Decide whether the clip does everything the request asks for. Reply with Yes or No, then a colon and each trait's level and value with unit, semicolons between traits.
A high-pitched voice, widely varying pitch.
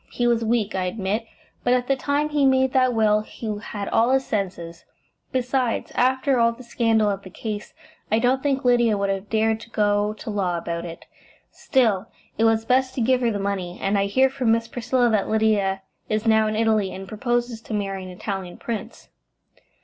No: high, 220 Hz; average, 3.5 semitones